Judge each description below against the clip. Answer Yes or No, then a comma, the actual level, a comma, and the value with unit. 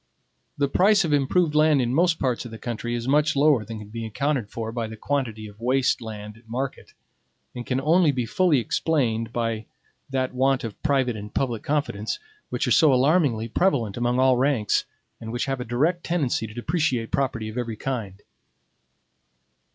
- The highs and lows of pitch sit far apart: No, average, 4.1 semitones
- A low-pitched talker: Yes, low, 125 Hz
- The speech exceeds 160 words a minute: Yes, average, 185 wpm